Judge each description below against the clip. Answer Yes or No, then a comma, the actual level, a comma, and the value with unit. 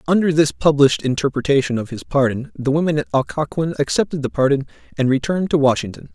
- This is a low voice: No, medium, 145 Hz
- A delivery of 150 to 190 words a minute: Yes, average, 175 wpm